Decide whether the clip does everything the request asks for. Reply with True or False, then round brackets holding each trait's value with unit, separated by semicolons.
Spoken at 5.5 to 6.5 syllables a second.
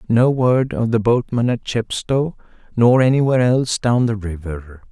False (4.7 syllables/s)